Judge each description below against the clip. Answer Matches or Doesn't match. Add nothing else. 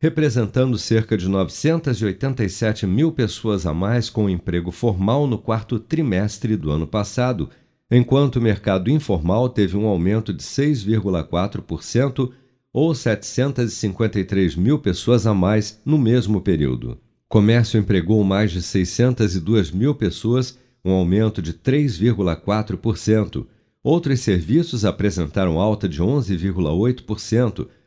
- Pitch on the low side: Matches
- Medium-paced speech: Doesn't match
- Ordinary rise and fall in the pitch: Matches